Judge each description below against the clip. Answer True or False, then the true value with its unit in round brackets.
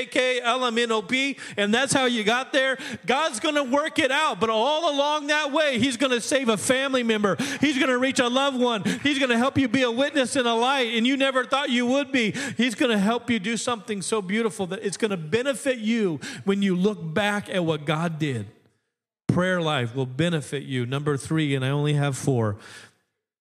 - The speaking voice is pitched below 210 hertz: False (235 Hz)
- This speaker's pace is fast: True (230 wpm)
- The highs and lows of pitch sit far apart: True (5.8 semitones)